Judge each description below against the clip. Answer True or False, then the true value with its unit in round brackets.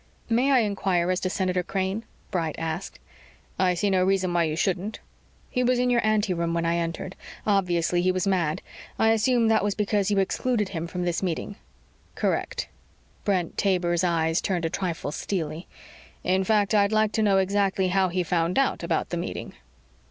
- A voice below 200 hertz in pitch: True (190 Hz)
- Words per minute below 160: False (180 wpm)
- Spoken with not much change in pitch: False (3.0 semitones)